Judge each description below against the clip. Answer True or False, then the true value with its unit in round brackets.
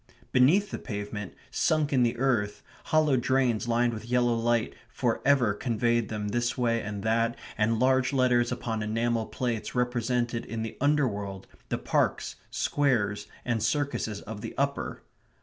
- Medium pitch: False (120 Hz)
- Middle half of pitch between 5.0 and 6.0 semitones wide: False (2.6 semitones)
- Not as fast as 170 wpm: True (150 wpm)